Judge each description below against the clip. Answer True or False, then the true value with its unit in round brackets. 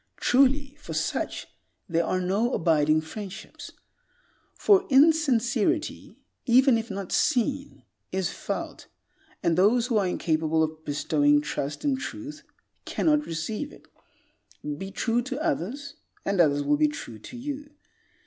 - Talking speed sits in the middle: False (130 wpm)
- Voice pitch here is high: True (225 Hz)